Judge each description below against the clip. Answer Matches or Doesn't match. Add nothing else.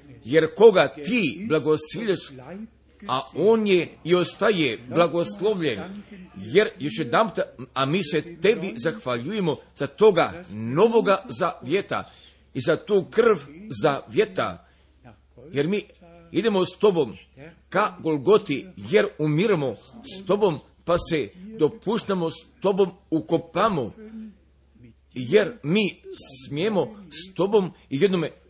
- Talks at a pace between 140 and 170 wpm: Doesn't match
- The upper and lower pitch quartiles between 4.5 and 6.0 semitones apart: Matches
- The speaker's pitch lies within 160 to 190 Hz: Matches